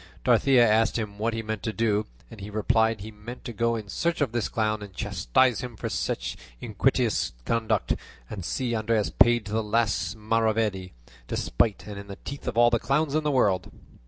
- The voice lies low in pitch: Yes, low, 110 Hz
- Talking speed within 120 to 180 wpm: No, average, 200 wpm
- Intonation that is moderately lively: No, narrow, 2.1 semitones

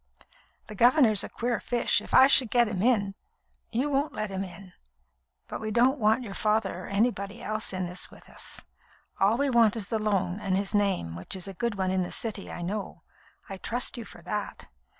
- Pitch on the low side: No, high, 210 Hz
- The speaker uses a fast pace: Yes, fast, 210 wpm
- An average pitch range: Yes, average, 3.4 semitones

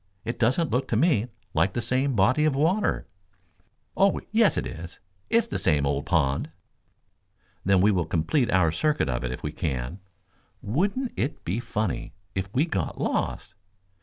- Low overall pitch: Yes, low, 110 Hz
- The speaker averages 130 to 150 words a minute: No, average, 165 wpm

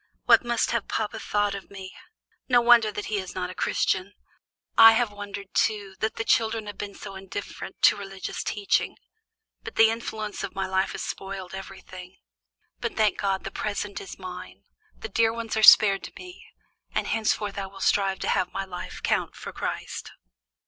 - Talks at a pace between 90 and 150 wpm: No, average, 185 wpm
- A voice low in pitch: No, high, 200 Hz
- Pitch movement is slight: Yes, narrow, 2.2 semitones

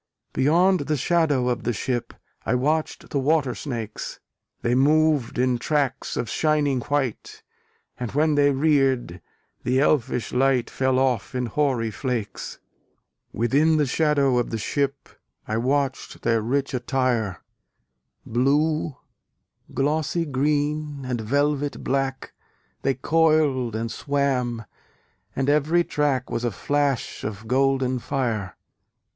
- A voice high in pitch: No, low, 135 Hz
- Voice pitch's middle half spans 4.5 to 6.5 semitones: No, average, 3.2 semitones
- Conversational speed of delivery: No, slow, 125 wpm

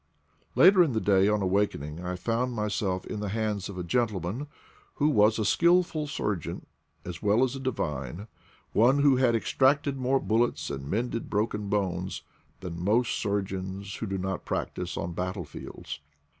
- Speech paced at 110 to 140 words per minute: No, average, 170 wpm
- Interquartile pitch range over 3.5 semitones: Yes, average, 4.8 semitones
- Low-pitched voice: Yes, low, 105 Hz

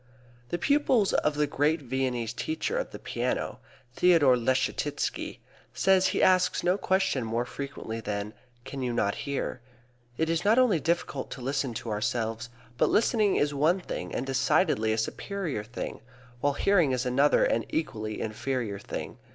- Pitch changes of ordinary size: No, wide, 6.8 semitones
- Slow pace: No, average, 160 wpm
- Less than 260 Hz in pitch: Yes, medium, 140 Hz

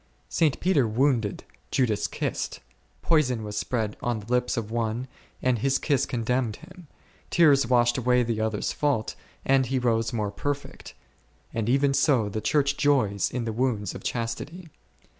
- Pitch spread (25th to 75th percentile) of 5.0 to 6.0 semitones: No, average, 3.7 semitones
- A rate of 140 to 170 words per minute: Yes, average, 160 wpm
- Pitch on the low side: Yes, low, 125 Hz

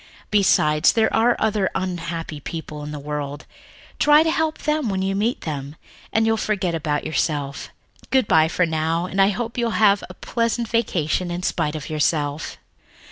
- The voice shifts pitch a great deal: Yes, wide, 6.5 semitones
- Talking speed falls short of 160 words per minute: No, average, 175 wpm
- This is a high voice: No, medium, 180 Hz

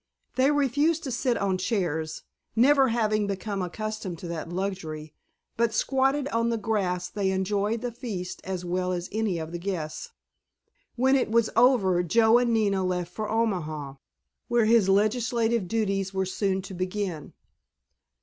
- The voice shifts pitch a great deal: No, average, 4.1 semitones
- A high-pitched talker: Yes, high, 205 Hz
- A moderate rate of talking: Yes, average, 155 wpm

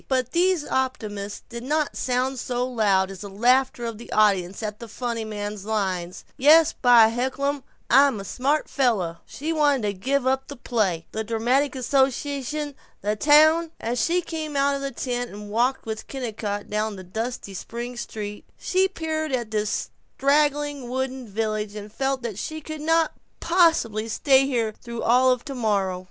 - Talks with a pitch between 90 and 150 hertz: No, high, 245 Hz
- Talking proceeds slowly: No, average, 170 wpm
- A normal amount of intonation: Yes, average, 4.6 semitones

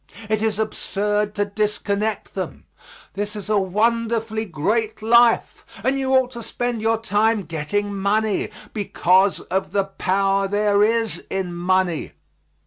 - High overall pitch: Yes, high, 210 Hz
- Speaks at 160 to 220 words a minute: No, slow, 135 wpm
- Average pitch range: No, narrow, 2.3 semitones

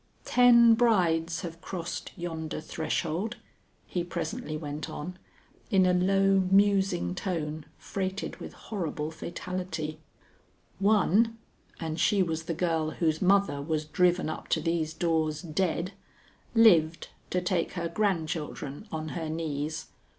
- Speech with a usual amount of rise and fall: Yes, average, 3.3 semitones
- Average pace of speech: No, slow, 125 wpm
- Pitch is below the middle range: No, medium, 170 Hz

